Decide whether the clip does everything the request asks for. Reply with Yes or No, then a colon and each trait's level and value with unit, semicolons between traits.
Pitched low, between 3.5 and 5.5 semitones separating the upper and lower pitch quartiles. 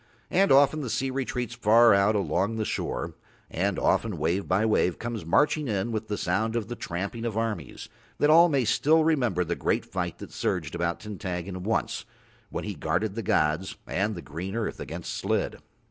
Yes: low, 110 Hz; average, 4.4 semitones